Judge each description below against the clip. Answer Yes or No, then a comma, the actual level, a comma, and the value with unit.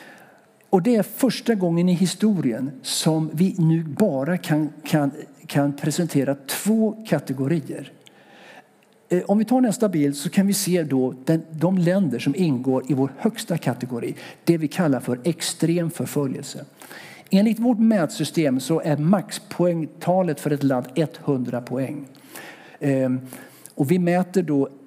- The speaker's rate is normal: Yes, average, 140 wpm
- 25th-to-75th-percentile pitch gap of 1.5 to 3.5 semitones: No, average, 5.1 semitones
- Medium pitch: Yes, medium, 165 Hz